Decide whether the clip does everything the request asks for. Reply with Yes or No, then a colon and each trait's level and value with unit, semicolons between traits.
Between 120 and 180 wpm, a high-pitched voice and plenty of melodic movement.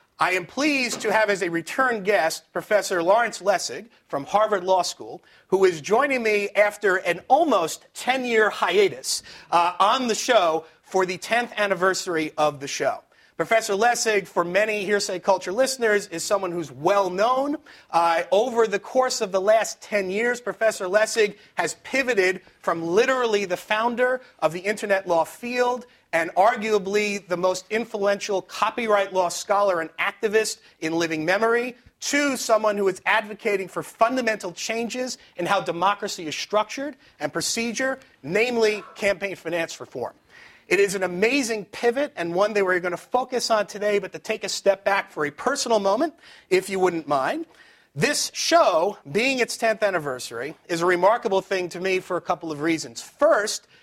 No: average, 165 wpm; high, 205 Hz; average, 4.1 semitones